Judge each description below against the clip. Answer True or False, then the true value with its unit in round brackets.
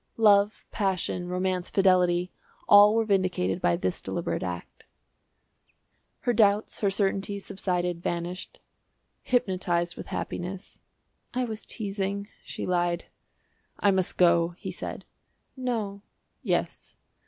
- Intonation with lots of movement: False (2.6 semitones)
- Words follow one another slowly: True (110 wpm)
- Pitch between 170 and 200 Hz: True (190 Hz)